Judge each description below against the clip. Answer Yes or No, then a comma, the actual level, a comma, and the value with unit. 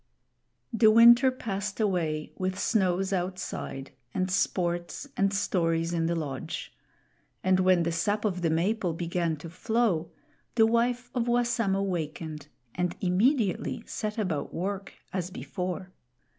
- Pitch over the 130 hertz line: Yes, medium, 185 Hz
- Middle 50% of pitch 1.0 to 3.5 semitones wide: No, average, 4.0 semitones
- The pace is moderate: No, slow, 130 wpm